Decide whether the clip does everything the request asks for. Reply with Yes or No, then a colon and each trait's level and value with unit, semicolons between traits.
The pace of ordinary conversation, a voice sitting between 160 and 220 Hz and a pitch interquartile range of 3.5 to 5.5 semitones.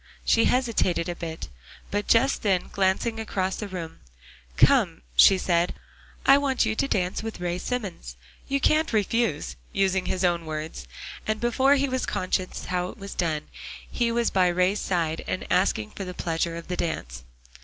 Yes: average, 175 wpm; medium, 185 Hz; average, 4.7 semitones